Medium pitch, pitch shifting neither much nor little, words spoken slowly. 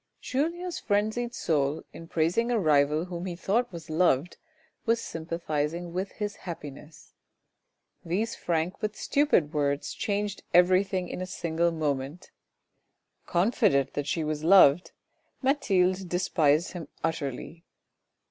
Yes: medium, 175 Hz; average, 4.4 semitones; slow, 120 wpm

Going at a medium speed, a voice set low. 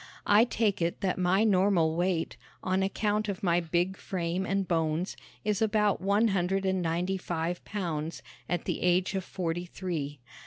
No: average, 165 wpm; medium, 185 Hz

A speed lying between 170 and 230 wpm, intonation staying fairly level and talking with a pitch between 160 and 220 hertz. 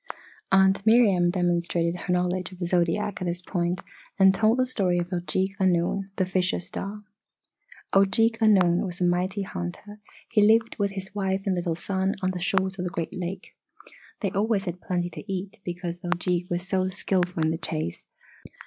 Yes: average, 180 wpm; narrow, 2.0 semitones; medium, 185 Hz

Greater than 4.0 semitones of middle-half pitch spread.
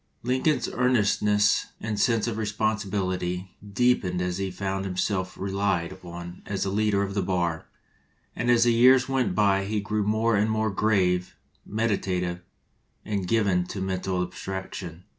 No: average, 2.9 semitones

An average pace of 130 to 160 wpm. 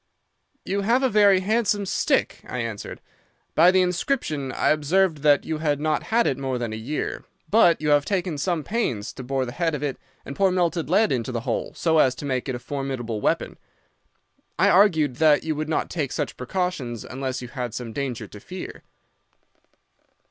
No: average, 195 wpm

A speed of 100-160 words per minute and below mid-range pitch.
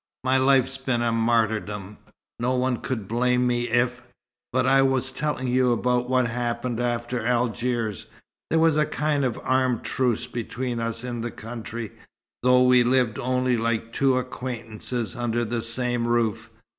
Yes: average, 155 wpm; low, 120 Hz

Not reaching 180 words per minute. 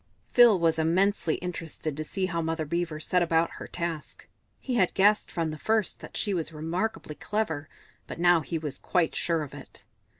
No: average, 190 wpm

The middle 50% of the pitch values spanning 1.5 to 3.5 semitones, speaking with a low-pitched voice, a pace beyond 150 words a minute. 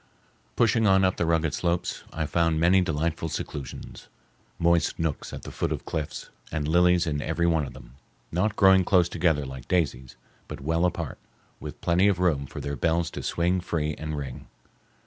Yes: average, 2.9 semitones; very low, 85 Hz; average, 180 wpm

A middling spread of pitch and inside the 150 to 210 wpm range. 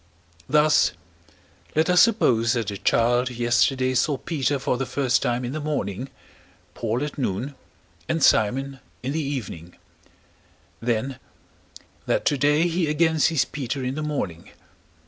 No: average, 3.8 semitones; average, 140 wpm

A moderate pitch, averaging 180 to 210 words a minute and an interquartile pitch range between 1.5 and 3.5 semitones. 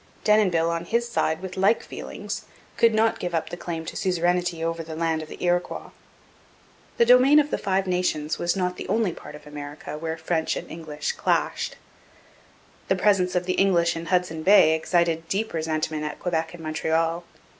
Yes: medium, 170 Hz; average, 185 wpm; average, 2.7 semitones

